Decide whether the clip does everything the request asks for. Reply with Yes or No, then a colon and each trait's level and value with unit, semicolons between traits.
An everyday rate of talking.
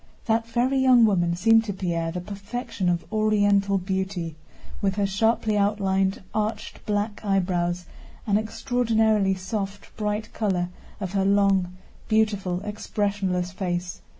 No: slow, 130 wpm